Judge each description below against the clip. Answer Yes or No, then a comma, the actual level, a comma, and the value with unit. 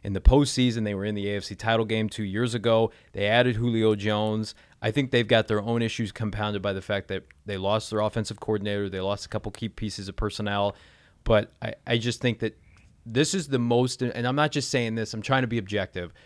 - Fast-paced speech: Yes, fast, 235 wpm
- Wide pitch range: No, average, 2.8 semitones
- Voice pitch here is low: Yes, low, 110 Hz